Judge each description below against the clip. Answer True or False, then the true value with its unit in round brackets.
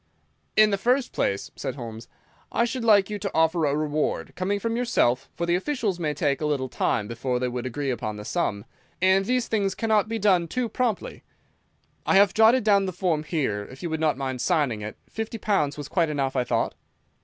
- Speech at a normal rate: False (210 wpm)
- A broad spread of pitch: True (7.8 semitones)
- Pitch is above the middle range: False (170 Hz)